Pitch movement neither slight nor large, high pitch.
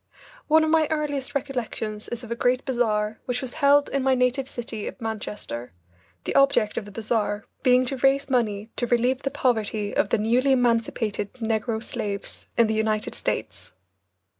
Yes: average, 3.5 semitones; high, 240 Hz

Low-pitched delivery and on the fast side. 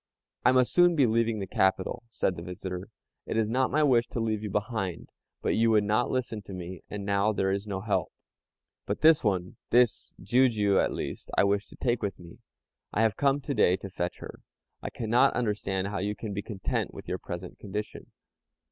Yes: low, 105 Hz; fast, 210 wpm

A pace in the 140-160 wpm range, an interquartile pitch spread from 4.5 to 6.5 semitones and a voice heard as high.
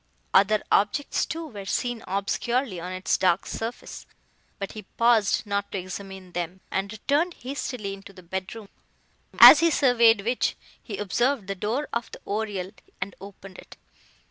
No: average, 155 wpm; average, 3.8 semitones; high, 205 Hz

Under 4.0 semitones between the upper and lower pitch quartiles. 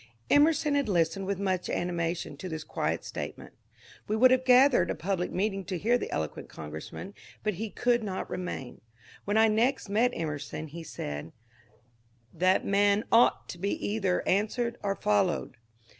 No: average, 4.4 semitones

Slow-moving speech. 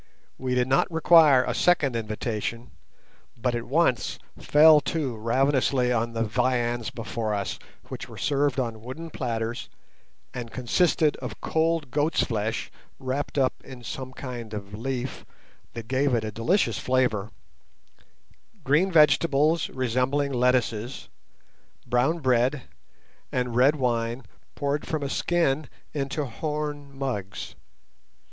Yes: slow, 125 wpm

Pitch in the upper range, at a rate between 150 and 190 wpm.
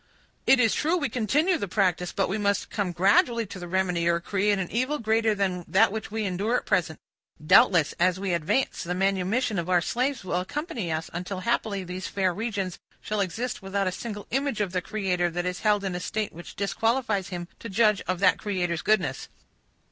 No: high, 195 Hz; fast, 205 wpm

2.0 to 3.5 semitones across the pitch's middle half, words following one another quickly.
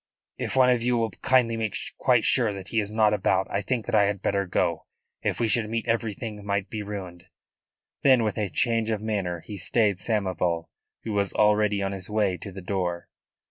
Yes: narrow, 2.6 semitones; fast, 210 wpm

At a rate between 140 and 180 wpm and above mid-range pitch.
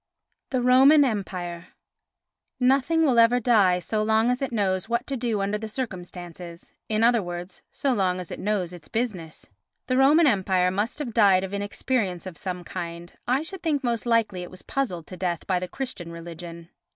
No: average, 190 wpm; high, 205 Hz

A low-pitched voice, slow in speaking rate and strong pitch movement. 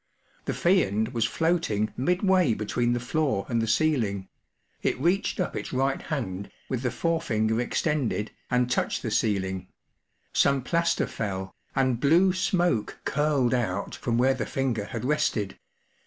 No: low, 125 Hz; average, 145 wpm; wide, 5.9 semitones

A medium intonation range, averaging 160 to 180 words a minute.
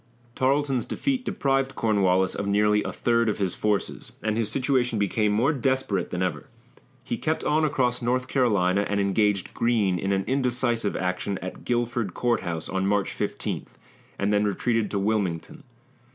Yes: average, 4.1 semitones; average, 165 wpm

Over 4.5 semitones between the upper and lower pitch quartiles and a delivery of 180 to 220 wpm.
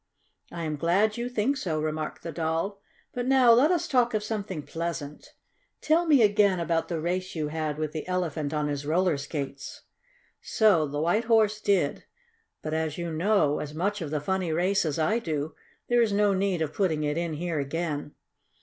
Yes: average, 5.1 semitones; average, 195 wpm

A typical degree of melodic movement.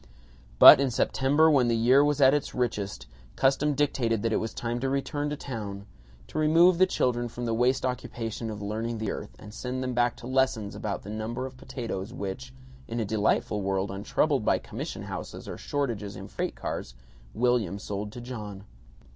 Yes: average, 3.9 semitones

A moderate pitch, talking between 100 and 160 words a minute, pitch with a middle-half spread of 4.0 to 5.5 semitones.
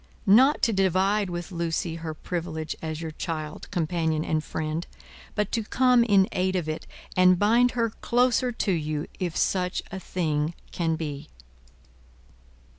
Yes: medium, 175 Hz; average, 150 wpm; average, 4.4 semitones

